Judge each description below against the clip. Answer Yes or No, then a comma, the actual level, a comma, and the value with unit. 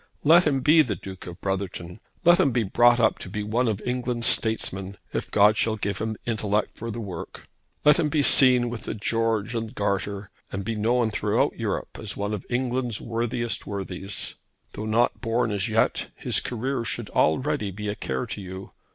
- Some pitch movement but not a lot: Yes, average, 3.1 semitones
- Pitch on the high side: No, low, 110 Hz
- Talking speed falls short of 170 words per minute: No, average, 195 wpm